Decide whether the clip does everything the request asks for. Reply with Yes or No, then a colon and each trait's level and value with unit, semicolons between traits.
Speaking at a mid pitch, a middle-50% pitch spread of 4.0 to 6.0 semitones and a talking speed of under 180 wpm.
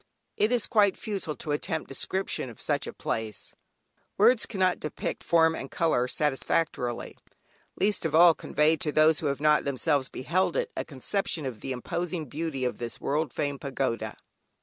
Yes: medium, 155 Hz; average, 4.8 semitones; average, 170 wpm